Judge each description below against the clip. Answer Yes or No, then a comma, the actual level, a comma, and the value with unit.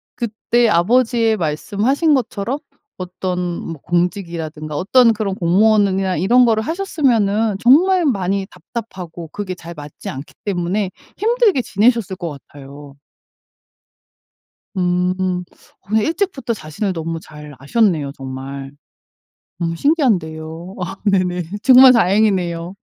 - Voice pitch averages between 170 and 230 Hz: Yes, high, 190 Hz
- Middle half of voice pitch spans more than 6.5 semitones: No, wide, 5.4 semitones